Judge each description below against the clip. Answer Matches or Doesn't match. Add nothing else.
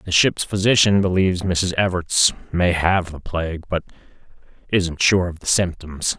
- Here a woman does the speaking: Doesn't match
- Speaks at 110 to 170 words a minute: Matches